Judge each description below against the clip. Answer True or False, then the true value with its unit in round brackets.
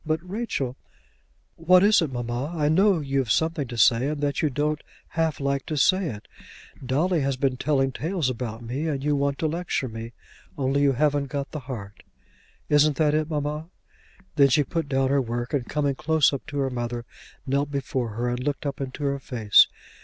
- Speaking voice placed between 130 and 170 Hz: True (140 Hz)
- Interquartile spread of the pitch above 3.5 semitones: False (3.0 semitones)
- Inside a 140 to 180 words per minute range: False (200 wpm)